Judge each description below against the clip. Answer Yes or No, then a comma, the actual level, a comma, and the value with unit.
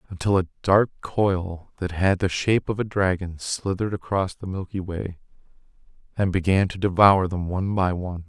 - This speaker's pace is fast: No, average, 175 wpm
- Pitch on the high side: No, very low, 95 Hz